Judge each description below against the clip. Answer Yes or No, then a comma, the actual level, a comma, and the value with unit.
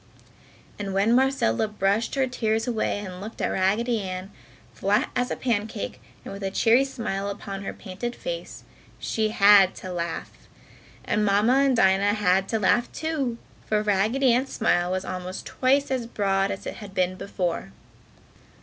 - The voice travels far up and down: No, average, 3.7 semitones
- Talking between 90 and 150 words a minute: No, average, 165 wpm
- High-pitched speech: Yes, high, 205 Hz